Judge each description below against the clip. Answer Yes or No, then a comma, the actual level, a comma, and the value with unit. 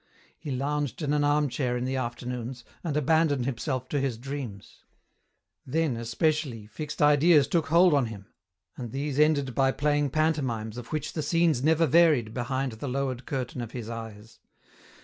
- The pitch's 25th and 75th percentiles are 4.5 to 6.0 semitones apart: No, average, 3.6 semitones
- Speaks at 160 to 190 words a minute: Yes, average, 170 wpm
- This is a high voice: No, low, 135 Hz